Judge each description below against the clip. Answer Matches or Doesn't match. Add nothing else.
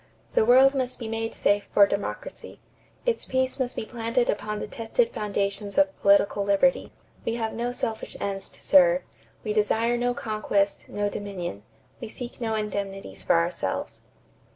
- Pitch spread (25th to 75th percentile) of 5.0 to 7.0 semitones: Doesn't match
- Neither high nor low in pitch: Doesn't match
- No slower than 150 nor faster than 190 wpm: Matches